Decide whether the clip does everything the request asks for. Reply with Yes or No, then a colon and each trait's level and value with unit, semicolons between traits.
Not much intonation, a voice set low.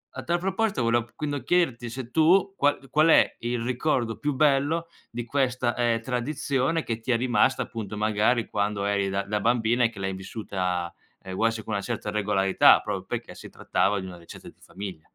No: average, 4.9 semitones; low, 120 Hz